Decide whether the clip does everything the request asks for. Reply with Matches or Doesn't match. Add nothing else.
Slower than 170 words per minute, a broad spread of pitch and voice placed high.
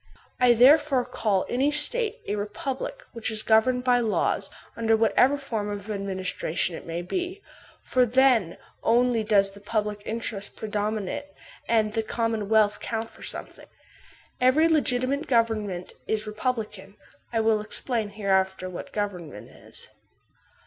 Doesn't match